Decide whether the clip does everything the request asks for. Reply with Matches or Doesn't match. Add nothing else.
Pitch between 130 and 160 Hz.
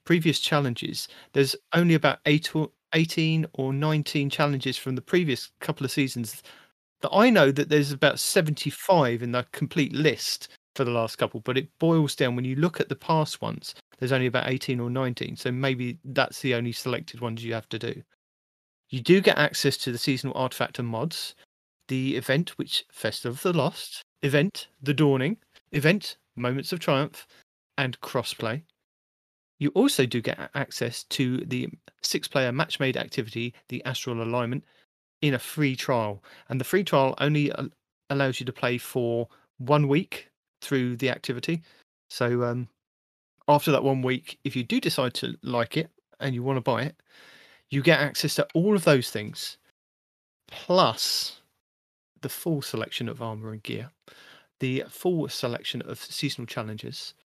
Matches